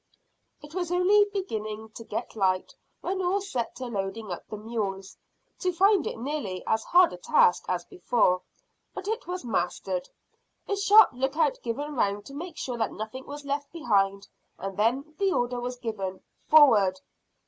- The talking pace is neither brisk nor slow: Yes, average, 170 wpm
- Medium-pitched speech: No, high, 245 Hz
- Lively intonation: Yes, wide, 8.6 semitones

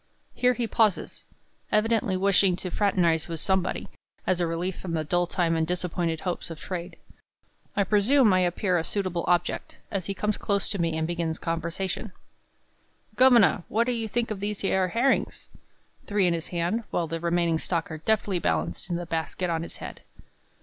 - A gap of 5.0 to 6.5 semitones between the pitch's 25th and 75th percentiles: No, average, 3.3 semitones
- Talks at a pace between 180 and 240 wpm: Yes, average, 185 wpm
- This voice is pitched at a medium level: Yes, medium, 180 Hz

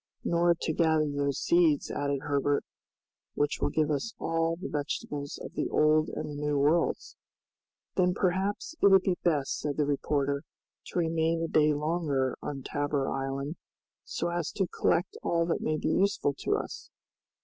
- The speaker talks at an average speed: Yes, average, 170 wpm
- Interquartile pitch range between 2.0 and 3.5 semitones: Yes, average, 2.9 semitones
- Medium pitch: Yes, medium, 155 Hz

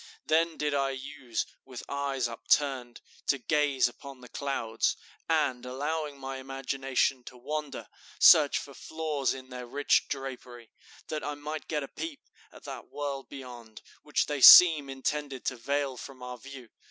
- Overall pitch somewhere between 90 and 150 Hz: Yes, low, 135 Hz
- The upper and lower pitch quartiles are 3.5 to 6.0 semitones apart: No, narrow, 2.5 semitones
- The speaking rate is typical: Yes, average, 155 wpm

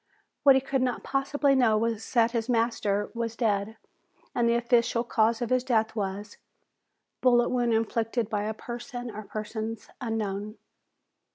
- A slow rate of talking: No, average, 155 wpm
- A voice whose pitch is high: Yes, high, 230 Hz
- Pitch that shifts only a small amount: Yes, narrow, 2.0 semitones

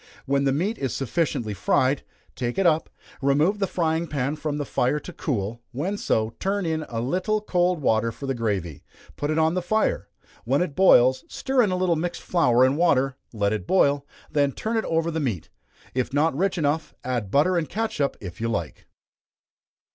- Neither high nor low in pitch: Yes, medium, 145 Hz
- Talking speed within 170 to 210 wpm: Yes, average, 195 wpm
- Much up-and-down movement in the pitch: Yes, wide, 5.8 semitones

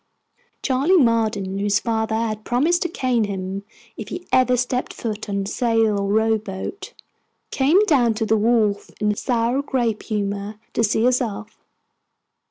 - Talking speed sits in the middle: Yes, average, 155 wpm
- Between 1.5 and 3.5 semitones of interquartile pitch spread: Yes, average, 3.2 semitones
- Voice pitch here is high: Yes, high, 225 Hz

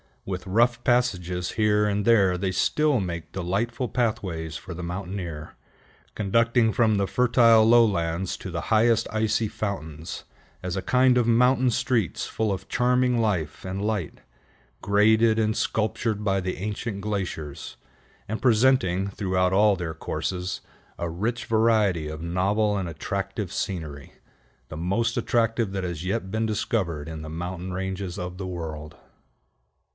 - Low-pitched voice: Yes, low, 100 Hz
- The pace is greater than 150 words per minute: No, average, 145 wpm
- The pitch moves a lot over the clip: No, average, 4.0 semitones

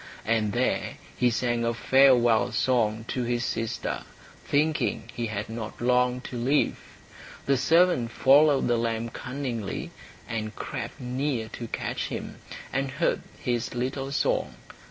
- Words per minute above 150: No, slow, 135 wpm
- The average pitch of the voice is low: Yes, low, 120 Hz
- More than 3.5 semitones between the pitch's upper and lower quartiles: No, narrow, 2.5 semitones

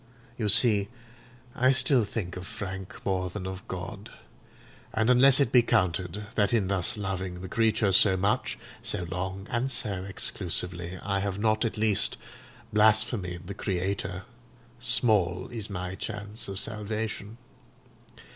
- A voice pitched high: No, low, 100 Hz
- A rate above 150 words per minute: No, average, 140 wpm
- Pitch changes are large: No, average, 2.9 semitones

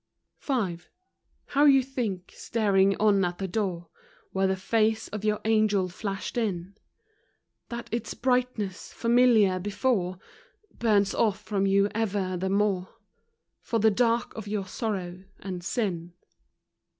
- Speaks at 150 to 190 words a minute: No, slow, 135 wpm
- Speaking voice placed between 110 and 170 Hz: No, high, 205 Hz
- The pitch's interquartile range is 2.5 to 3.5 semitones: Yes, average, 3.0 semitones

